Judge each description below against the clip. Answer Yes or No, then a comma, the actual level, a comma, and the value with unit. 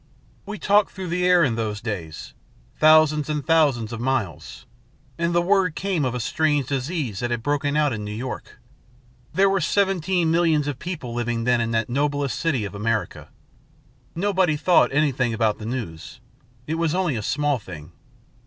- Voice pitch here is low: No, medium, 145 Hz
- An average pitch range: No, wide, 6.4 semitones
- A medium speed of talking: Yes, average, 175 wpm